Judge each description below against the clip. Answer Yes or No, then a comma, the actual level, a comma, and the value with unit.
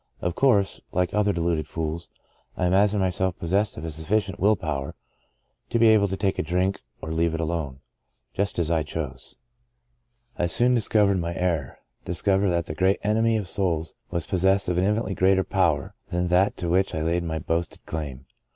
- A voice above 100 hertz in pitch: No, very low, 90 Hz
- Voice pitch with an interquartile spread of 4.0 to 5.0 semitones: No, average, 3.2 semitones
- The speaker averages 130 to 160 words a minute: No, average, 195 wpm